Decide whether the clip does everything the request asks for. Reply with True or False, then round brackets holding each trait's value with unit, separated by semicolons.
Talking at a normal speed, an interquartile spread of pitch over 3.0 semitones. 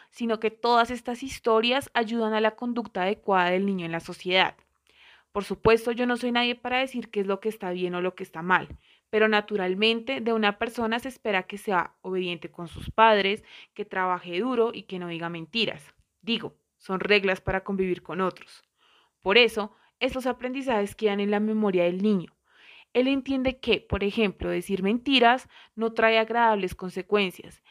True (180 wpm; 3.9 semitones)